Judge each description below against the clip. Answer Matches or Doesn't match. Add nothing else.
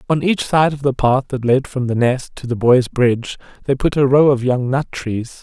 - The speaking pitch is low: Matches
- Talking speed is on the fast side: Matches